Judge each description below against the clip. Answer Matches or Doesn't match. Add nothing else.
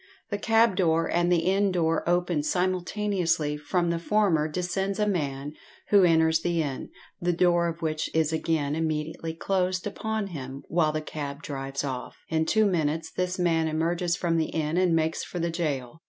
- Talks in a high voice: Doesn't match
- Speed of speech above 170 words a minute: Matches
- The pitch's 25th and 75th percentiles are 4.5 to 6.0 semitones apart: Doesn't match